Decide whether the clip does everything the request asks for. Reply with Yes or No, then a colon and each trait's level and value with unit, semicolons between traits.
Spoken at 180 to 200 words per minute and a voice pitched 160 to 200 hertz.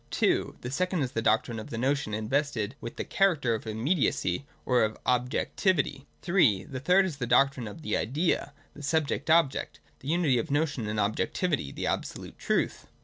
No: average, 190 wpm; low, 135 Hz